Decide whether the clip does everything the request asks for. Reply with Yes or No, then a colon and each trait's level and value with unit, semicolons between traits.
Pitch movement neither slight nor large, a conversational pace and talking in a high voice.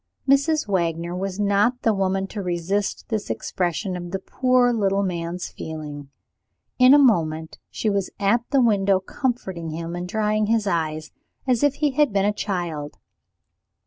Yes: average, 4.7 semitones; average, 160 wpm; high, 195 Hz